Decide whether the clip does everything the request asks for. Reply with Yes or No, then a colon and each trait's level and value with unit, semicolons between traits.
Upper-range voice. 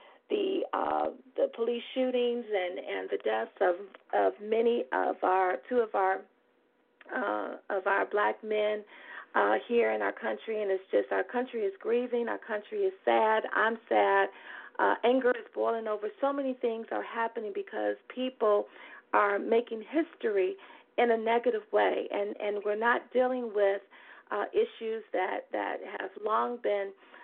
Yes: high, 230 Hz